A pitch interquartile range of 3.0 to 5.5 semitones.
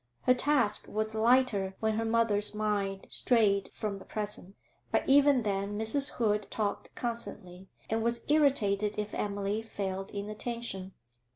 No: narrow, 2.6 semitones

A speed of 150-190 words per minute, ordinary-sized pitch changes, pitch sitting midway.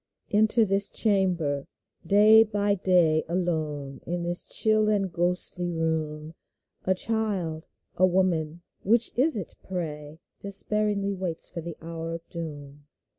No: average, 140 wpm; average, 3.9 semitones; medium, 175 Hz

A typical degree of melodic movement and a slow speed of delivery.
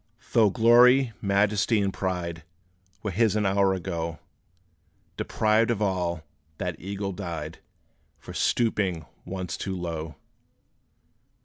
Yes: average, 3.5 semitones; slow, 110 wpm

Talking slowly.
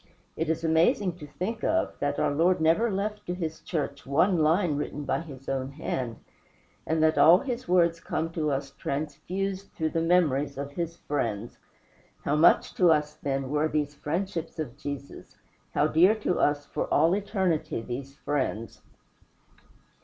No: average, 165 wpm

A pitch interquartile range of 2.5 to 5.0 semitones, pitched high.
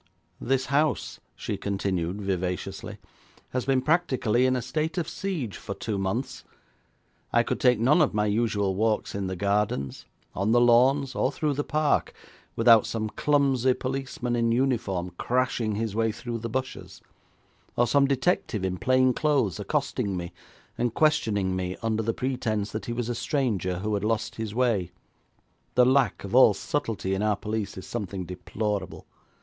No: average, 4.2 semitones; low, 115 Hz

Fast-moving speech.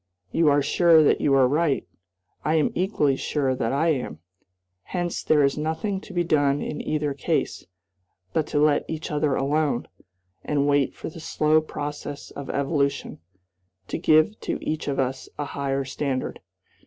No: average, 165 wpm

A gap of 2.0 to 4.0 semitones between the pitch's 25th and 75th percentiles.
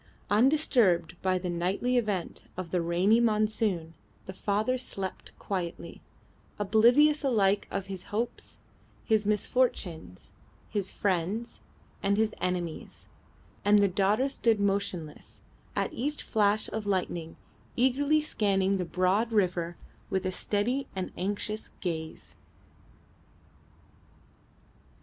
Yes: average, 3.6 semitones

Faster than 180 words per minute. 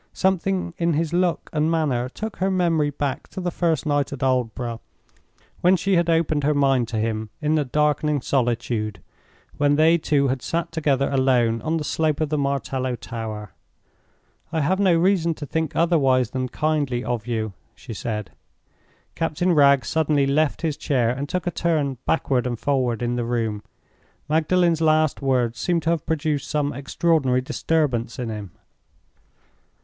No: average, 165 wpm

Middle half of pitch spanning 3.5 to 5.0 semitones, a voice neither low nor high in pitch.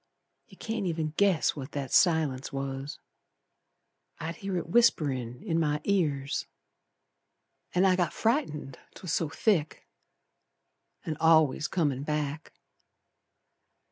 Yes: average, 4.2 semitones; medium, 160 Hz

